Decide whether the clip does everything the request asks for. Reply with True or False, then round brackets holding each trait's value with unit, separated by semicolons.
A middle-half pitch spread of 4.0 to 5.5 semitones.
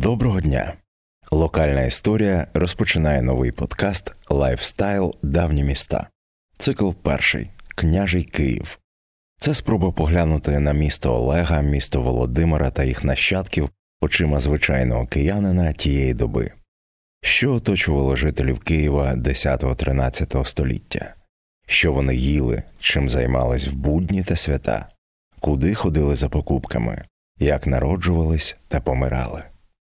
True (4.5 semitones)